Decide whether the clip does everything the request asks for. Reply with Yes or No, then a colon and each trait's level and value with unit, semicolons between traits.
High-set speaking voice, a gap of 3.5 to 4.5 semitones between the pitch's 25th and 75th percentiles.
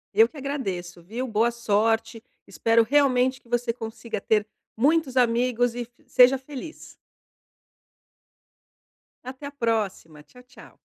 No: high, 235 Hz; narrow, 2.6 semitones